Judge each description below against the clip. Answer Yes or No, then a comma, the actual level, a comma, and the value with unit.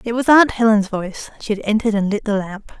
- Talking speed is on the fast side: Yes, fast, 255 wpm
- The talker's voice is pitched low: No, high, 215 Hz